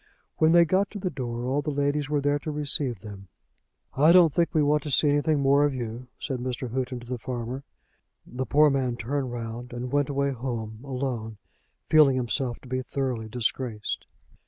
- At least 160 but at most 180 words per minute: No, average, 195 wpm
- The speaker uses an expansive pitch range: No, average, 3.1 semitones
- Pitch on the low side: Yes, low, 130 Hz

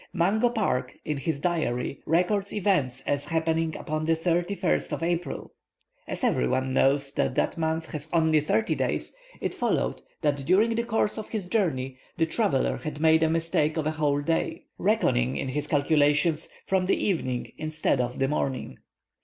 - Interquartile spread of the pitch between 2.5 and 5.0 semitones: Yes, average, 3.8 semitones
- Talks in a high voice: No, medium, 160 Hz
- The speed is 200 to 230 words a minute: No, average, 170 wpm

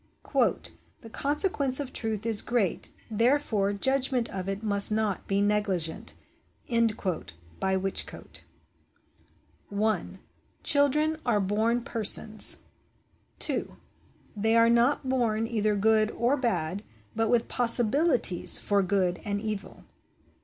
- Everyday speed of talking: No, slow, 110 wpm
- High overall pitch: Yes, high, 220 Hz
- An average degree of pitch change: Yes, average, 3.1 semitones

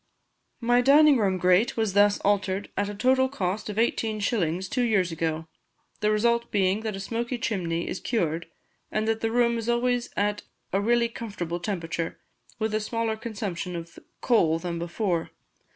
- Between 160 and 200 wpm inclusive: Yes, average, 170 wpm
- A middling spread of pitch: Yes, average, 4.3 semitones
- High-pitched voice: Yes, high, 210 Hz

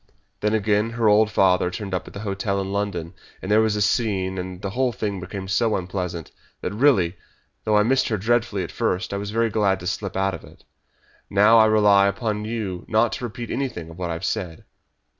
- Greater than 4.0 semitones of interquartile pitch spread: No, average, 2.7 semitones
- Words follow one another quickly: Yes, fast, 220 wpm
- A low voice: Yes, low, 100 Hz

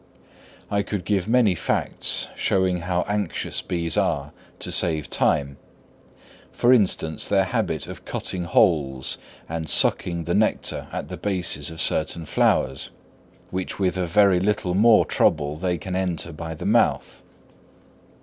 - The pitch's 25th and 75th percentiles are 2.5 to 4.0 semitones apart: Yes, average, 3.3 semitones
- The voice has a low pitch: Yes, very low, 90 Hz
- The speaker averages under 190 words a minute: Yes, average, 140 wpm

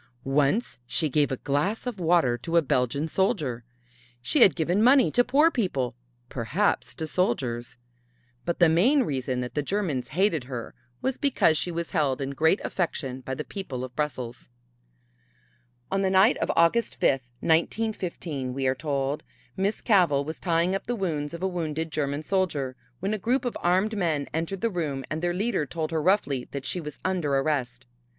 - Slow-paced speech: No, average, 180 wpm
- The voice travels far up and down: Yes, wide, 5.9 semitones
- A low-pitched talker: No, medium, 160 Hz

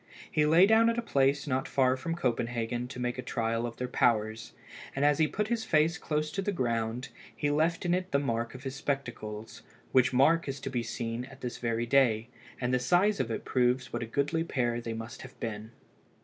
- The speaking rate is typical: No, fast, 220 wpm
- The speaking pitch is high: No, low, 130 Hz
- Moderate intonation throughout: Yes, average, 4.4 semitones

